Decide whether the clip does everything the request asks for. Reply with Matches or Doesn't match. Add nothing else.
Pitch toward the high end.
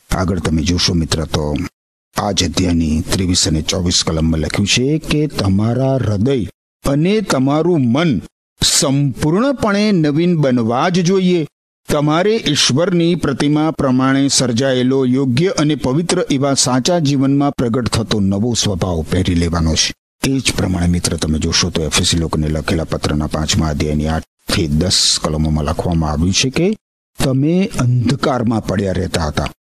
Doesn't match